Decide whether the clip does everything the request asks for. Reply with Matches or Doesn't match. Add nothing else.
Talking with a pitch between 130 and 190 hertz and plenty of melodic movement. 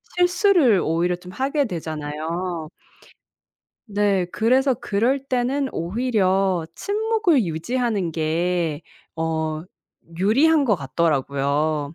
Matches